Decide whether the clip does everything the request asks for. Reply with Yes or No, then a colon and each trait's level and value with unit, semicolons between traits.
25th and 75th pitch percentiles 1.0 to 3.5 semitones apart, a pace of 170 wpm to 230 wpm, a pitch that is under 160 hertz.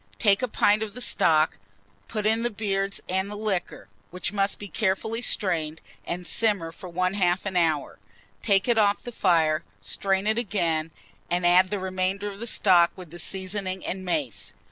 No: average, 2.9 semitones; average, 180 wpm; high, 190 Hz